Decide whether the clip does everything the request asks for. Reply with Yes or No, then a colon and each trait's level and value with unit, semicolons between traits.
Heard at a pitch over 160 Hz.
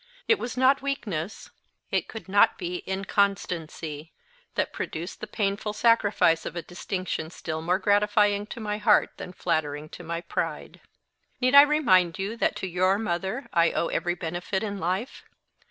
Yes: high, 190 Hz